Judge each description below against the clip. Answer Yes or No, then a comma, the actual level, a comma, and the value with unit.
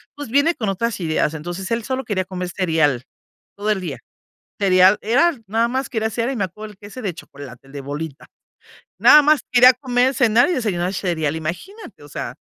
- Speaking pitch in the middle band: No, high, 205 Hz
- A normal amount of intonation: No, wide, 6.2 semitones